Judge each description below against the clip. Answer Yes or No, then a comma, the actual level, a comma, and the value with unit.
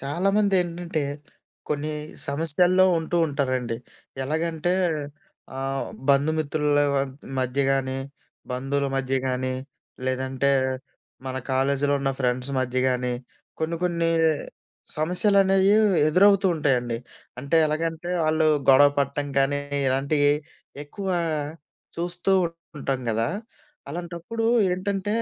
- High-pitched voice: No, medium, 145 Hz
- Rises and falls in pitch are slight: No, average, 4.3 semitones